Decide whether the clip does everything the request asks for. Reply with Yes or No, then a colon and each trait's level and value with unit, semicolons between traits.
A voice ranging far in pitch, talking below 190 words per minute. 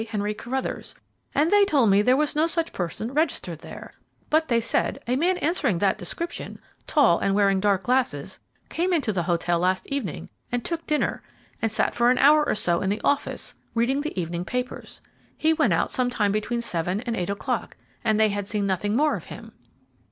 No: wide, 6.6 semitones; average, 200 wpm